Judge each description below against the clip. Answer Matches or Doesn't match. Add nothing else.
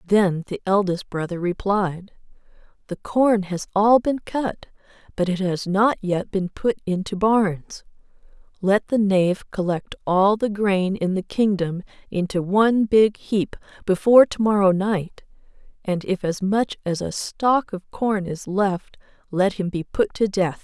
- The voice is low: Doesn't match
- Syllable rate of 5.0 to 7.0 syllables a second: Doesn't match